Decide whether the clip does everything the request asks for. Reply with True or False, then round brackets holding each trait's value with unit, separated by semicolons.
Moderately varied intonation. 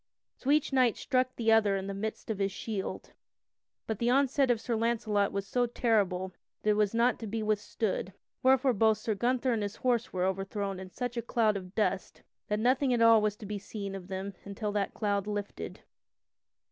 True (3.1 semitones)